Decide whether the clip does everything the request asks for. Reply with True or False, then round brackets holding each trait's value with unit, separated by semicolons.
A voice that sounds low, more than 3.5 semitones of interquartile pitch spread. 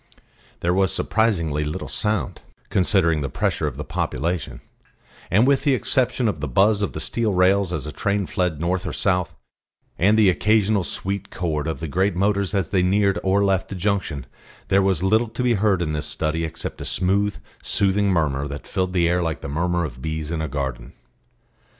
True (90 Hz; 4.1 semitones)